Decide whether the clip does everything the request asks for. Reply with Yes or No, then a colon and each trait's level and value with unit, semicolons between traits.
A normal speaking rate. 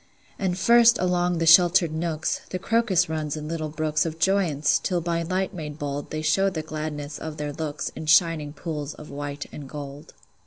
Yes: average, 190 wpm